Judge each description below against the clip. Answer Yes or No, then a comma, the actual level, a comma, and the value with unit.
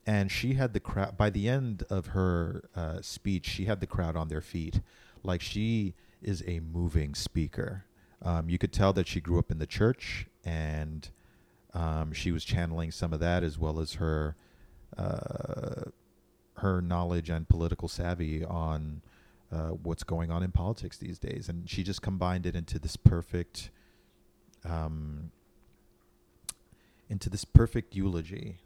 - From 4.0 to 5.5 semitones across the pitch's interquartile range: No, average, 3.4 semitones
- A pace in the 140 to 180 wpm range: Yes, average, 160 wpm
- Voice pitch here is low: Yes, very low, 90 Hz